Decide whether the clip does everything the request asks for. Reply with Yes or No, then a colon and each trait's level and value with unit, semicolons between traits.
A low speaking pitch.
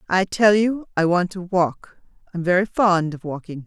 No: medium, 185 Hz